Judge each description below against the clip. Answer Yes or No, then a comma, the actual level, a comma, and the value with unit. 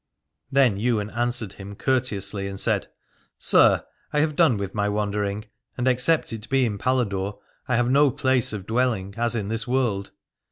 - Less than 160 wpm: No, average, 170 wpm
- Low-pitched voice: Yes, low, 115 Hz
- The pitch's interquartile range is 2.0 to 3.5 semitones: No, average, 4.0 semitones